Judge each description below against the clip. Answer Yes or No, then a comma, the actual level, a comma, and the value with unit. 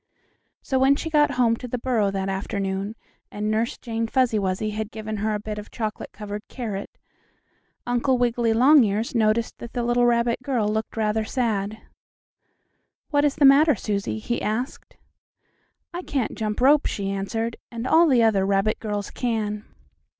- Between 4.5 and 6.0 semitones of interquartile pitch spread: No, average, 2.8 semitones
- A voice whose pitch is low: No, high, 225 Hz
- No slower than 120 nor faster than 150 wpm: No, average, 165 wpm